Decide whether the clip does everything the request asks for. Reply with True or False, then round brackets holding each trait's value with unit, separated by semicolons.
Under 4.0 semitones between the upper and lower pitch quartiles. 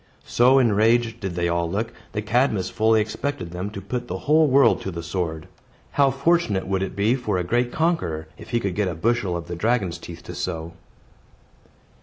False (5.4 semitones)